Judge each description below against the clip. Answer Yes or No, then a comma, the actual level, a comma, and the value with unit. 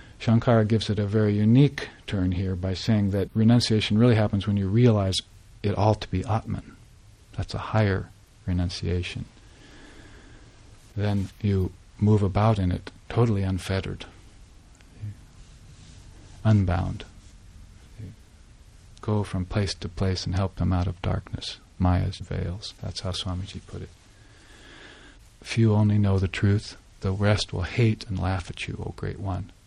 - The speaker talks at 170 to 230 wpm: No, average, 140 wpm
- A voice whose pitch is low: Yes, low, 100 Hz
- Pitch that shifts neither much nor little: No, narrow, 2.3 semitones